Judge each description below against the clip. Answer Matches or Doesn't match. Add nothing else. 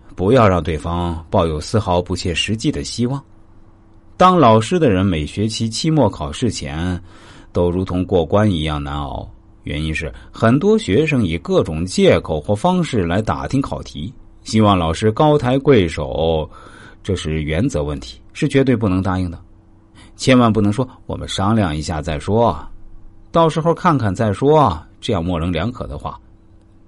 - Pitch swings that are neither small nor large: Matches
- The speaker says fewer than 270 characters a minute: Matches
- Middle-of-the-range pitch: Doesn't match